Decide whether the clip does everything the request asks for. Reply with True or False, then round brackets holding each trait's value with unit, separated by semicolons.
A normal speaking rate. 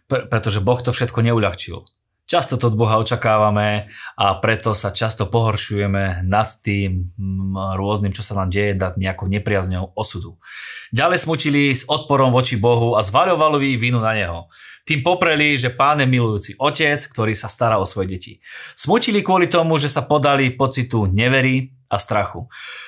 True (155 wpm)